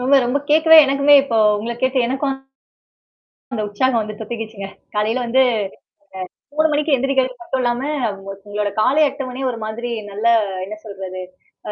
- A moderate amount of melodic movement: Yes, average, 4.0 semitones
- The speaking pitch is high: Yes, high, 245 Hz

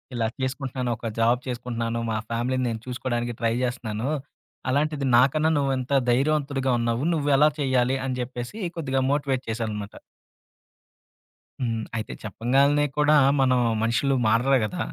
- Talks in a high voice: No, low, 125 Hz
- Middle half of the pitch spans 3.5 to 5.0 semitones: No, average, 2.8 semitones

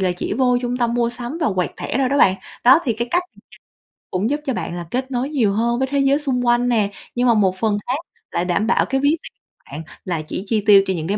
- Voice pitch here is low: No, high, 240 Hz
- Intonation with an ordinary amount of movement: Yes, average, 4.7 semitones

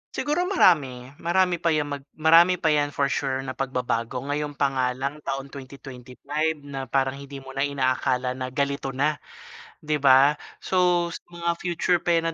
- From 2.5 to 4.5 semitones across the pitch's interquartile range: Yes, average, 3.3 semitones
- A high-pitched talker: No, medium, 140 Hz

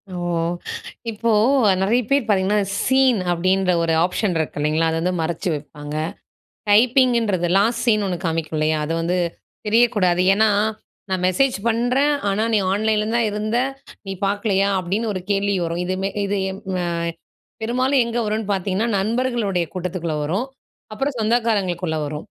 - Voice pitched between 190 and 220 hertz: Yes, high, 200 Hz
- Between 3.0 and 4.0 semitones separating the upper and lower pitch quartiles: No, average, 4.5 semitones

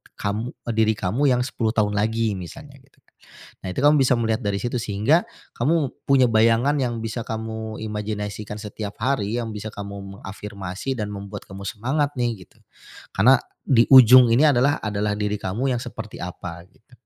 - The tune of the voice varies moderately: Yes, average, 3.5 semitones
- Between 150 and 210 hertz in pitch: No, low, 110 Hz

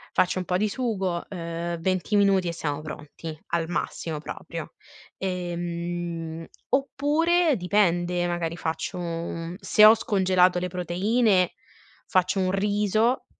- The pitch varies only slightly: No, average, 3.1 semitones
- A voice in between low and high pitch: Yes, medium, 180 Hz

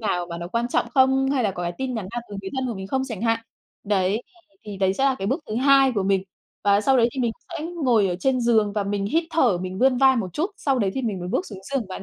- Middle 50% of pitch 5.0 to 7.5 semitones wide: Yes, average, 5.3 semitones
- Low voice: No, high, 225 Hz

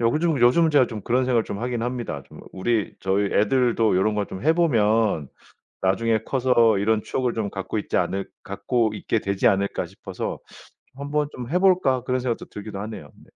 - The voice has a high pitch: No, low, 115 Hz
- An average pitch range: Yes, average, 4.0 semitones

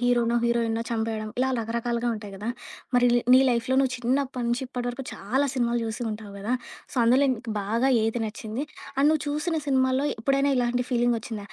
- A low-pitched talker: No, high, 240 Hz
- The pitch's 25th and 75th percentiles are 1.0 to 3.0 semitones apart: Yes, narrow, 2.4 semitones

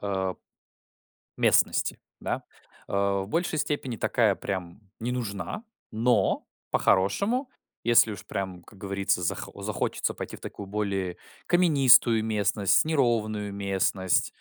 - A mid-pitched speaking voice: No, low, 105 Hz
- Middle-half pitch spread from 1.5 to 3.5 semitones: No, average, 4.0 semitones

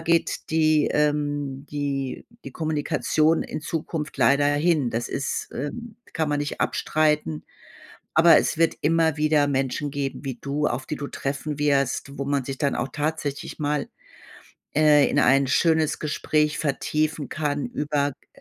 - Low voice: No, medium, 145 Hz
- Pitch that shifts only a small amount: Yes, narrow, 1.7 semitones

